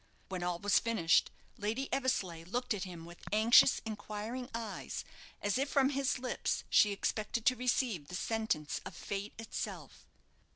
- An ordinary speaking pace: Yes, average, 155 wpm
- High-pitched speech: Yes, high, 215 Hz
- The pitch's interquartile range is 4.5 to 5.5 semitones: Yes, average, 4.8 semitones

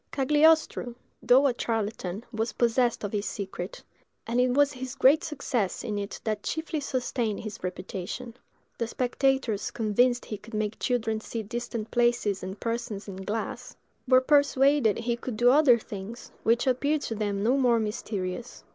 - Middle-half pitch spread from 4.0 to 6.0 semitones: No, average, 3.3 semitones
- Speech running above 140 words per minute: Yes, average, 160 wpm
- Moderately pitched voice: No, high, 235 Hz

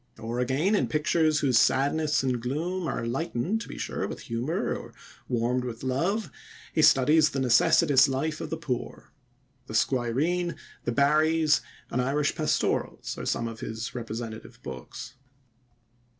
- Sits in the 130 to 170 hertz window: Yes, low, 135 Hz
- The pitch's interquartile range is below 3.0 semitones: No, average, 4.6 semitones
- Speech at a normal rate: Yes, average, 150 wpm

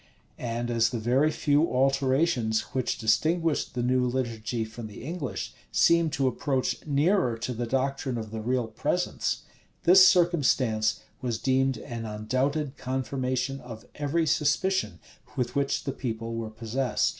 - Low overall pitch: Yes, low, 130 Hz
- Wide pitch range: No, average, 3.6 semitones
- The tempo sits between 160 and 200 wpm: No, average, 145 wpm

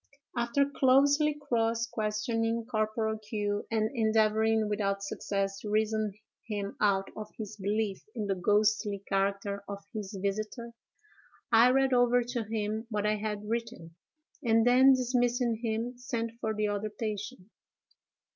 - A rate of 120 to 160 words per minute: Yes, slow, 135 wpm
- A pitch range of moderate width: No, narrow, 2.3 semitones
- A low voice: No, high, 220 Hz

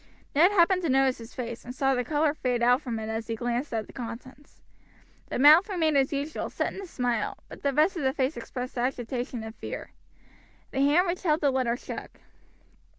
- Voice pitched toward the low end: No, very high, 265 Hz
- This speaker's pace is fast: Yes, fast, 215 wpm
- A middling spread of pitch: Yes, average, 4.0 semitones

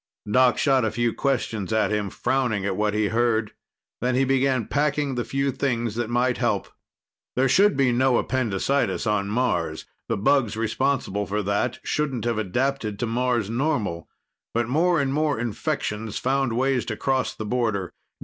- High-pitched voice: No, low, 120 Hz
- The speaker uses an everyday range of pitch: Yes, average, 3.8 semitones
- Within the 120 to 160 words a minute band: No, average, 170 wpm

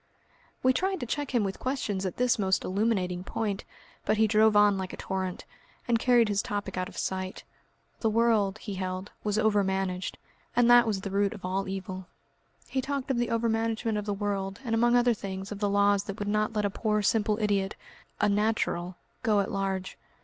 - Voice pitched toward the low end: No, high, 205 Hz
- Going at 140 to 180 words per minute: No, average, 200 wpm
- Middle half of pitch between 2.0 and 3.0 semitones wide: Yes, average, 2.7 semitones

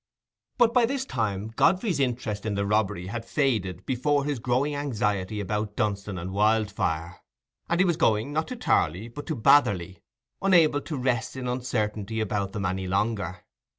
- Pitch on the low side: Yes, low, 110 Hz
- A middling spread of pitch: No, wide, 6.1 semitones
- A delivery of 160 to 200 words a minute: Yes, average, 165 wpm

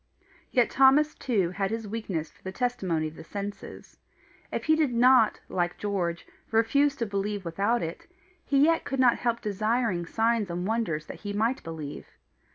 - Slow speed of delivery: No, average, 170 wpm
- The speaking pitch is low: No, high, 215 Hz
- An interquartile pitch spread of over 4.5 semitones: Yes, average, 5.2 semitones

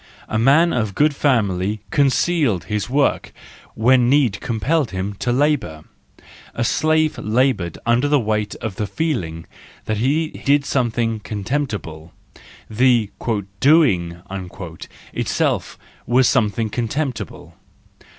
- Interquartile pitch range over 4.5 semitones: Yes, average, 5.2 semitones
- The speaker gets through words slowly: Yes, slow, 110 wpm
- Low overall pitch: Yes, low, 120 Hz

